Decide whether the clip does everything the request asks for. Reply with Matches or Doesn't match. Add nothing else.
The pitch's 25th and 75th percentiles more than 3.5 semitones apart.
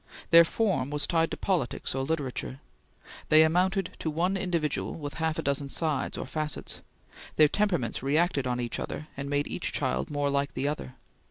Doesn't match